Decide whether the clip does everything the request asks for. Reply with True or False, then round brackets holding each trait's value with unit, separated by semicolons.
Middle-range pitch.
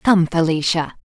True (170 Hz)